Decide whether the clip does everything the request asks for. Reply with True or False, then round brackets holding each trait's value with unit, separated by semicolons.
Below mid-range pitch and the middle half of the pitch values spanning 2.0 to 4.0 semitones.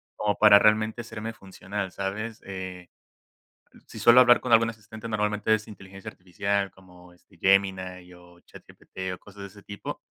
True (100 Hz; 2.6 semitones)